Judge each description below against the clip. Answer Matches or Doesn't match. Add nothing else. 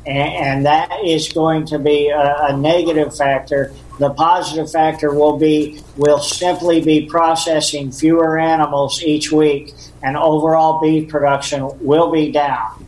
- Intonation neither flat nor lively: Doesn't match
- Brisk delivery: Doesn't match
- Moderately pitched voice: Matches